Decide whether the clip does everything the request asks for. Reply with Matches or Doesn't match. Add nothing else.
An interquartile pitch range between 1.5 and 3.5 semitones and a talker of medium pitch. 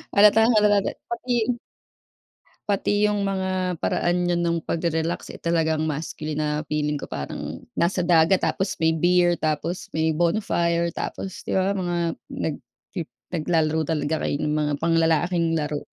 Matches